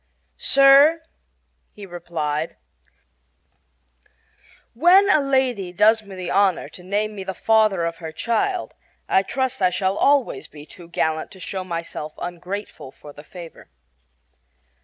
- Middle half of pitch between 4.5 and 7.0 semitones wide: Yes, wide, 5.5 semitones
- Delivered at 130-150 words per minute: Yes, slow, 135 wpm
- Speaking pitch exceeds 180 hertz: Yes, high, 190 Hz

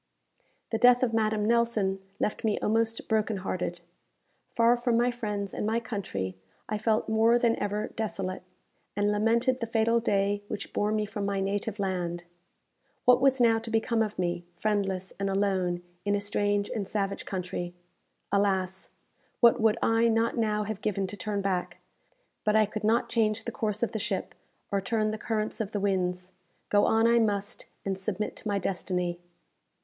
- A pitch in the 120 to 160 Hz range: No, high, 210 Hz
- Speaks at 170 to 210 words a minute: Yes, average, 175 wpm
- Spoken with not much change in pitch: Yes, narrow, 2.3 semitones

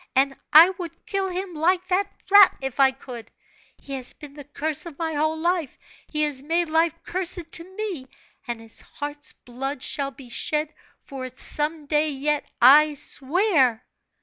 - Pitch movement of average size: Yes, average, 3.8 semitones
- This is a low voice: No, very high, 300 Hz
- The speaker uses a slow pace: No, average, 175 wpm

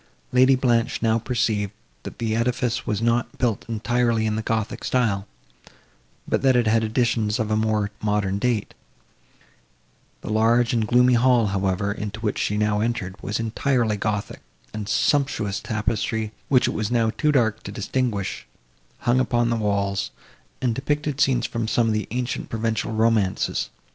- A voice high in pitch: No, low, 115 Hz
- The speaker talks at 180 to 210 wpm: No, average, 160 wpm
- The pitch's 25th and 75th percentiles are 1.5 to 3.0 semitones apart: Yes, narrow, 2.4 semitones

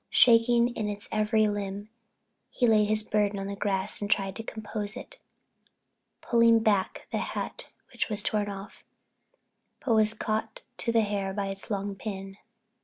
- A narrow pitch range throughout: Yes, narrow, 1.8 semitones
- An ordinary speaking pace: Yes, average, 160 wpm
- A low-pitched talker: No, high, 210 Hz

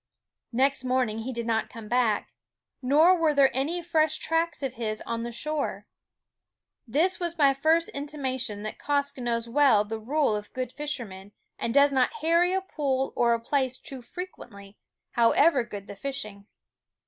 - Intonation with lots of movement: No, average, 4.5 semitones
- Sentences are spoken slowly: No, average, 170 wpm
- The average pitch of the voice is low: No, very high, 260 Hz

